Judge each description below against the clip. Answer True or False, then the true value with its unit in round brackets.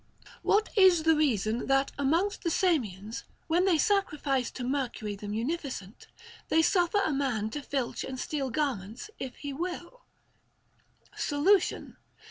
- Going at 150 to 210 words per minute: False (140 wpm)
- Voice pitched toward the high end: True (285 Hz)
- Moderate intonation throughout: False (5.9 semitones)